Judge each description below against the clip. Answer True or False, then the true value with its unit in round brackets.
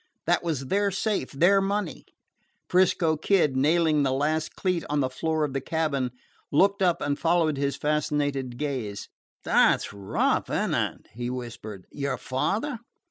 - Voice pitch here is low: False (150 Hz)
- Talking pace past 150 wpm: True (160 wpm)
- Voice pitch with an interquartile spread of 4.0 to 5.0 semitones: True (4.5 semitones)